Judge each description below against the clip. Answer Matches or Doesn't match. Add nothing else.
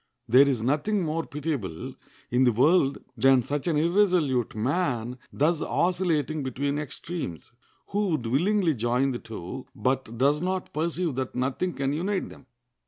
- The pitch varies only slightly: Doesn't match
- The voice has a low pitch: Doesn't match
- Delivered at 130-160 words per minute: Matches